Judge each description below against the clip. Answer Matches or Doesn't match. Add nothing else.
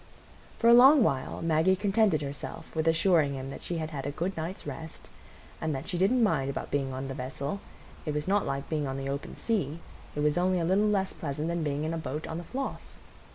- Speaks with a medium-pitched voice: Matches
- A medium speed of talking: Doesn't match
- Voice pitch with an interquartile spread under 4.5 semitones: Doesn't match